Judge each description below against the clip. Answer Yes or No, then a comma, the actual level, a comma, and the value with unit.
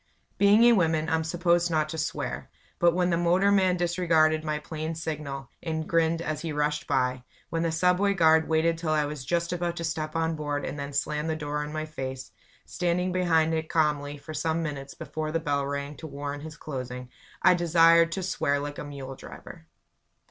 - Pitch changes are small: Yes, narrow, 2.3 semitones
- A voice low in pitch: No, medium, 160 Hz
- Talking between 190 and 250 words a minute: Yes, average, 200 wpm